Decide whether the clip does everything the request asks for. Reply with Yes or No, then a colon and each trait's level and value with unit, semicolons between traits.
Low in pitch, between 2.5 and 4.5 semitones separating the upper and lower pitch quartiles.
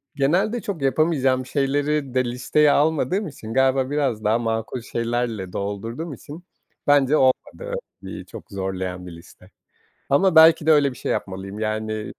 No: low, 130 Hz; wide, 5.6 semitones